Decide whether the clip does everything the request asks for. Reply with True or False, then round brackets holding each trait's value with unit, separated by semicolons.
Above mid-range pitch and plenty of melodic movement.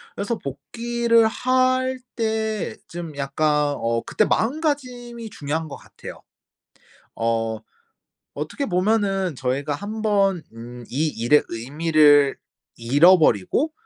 False (170 Hz; 8.2 semitones)